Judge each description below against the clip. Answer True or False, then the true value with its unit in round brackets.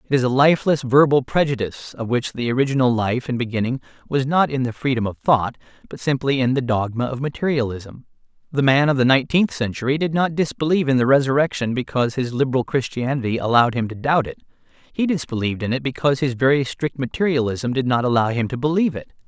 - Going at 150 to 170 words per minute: False (200 wpm)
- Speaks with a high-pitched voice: False (130 Hz)